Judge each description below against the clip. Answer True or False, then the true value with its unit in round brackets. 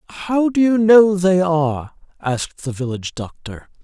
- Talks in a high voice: False (170 Hz)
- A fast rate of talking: False (155 wpm)